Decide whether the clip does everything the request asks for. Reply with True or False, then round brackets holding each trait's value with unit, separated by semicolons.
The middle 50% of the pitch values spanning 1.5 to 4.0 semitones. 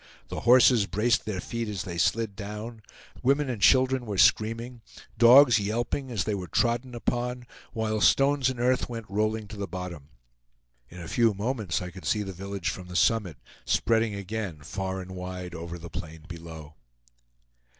False (4.5 semitones)